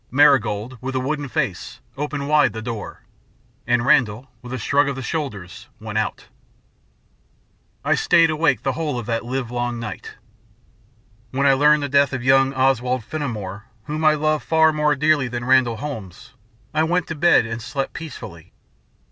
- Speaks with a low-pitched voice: Yes, low, 130 Hz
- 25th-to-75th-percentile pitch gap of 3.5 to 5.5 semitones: Yes, average, 3.9 semitones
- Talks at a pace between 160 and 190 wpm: Yes, average, 165 wpm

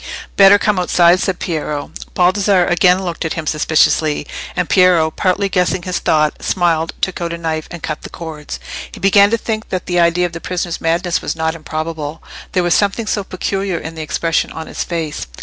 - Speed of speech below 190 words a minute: No, average, 200 wpm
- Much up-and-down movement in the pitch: No, narrow, 2.4 semitones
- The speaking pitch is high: No, medium, 175 Hz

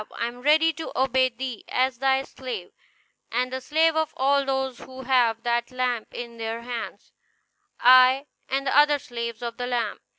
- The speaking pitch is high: Yes, very high, 255 Hz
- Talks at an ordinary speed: Yes, average, 175 wpm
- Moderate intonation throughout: No, narrow, 2.1 semitones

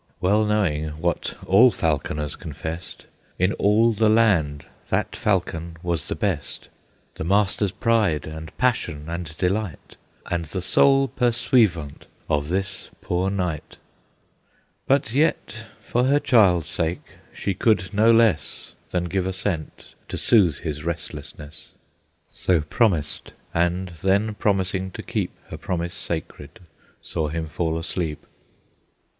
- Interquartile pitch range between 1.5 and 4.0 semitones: No, average, 4.8 semitones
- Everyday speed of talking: No, slow, 125 wpm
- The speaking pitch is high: No, very low, 90 Hz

